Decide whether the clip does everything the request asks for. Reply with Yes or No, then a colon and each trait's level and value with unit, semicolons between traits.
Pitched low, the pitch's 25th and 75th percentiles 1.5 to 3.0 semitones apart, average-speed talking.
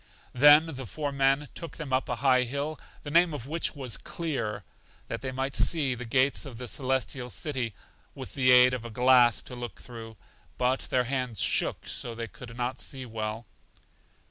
Yes: low, 130 Hz; narrow, 2.5 semitones; average, 190 wpm